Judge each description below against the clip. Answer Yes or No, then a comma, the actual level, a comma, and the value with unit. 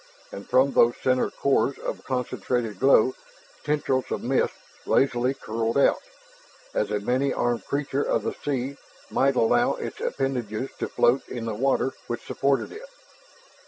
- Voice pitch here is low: Yes, low, 130 Hz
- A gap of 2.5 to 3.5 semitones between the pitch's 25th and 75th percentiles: Yes, average, 2.8 semitones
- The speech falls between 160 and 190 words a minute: No, average, 150 wpm